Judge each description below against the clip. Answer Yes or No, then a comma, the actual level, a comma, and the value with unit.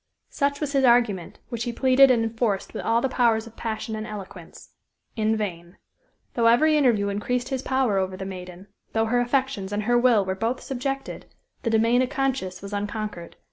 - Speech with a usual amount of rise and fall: Yes, average, 3.8 semitones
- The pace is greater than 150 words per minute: Yes, average, 190 wpm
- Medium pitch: No, high, 230 Hz